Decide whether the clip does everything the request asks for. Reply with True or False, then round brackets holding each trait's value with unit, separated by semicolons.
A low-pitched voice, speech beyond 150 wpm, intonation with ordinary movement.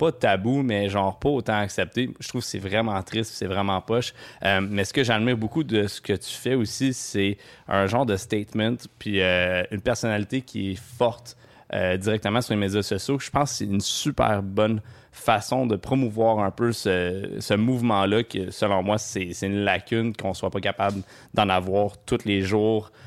True (110 Hz; 200 wpm; 3.4 semitones)